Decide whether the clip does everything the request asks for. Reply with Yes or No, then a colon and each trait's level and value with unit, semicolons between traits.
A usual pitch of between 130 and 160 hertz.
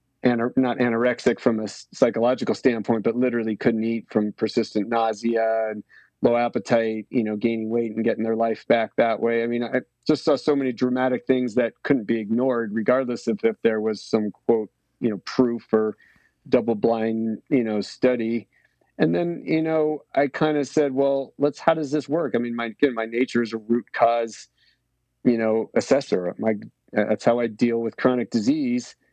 No: low, 120 Hz